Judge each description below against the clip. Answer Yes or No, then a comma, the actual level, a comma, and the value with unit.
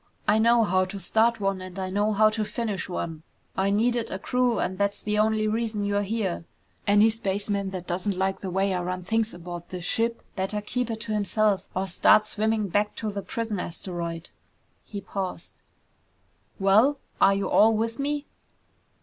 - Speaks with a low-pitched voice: No, high, 205 Hz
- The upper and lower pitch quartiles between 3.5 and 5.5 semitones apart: No, average, 2.7 semitones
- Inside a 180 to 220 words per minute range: Yes, average, 185 wpm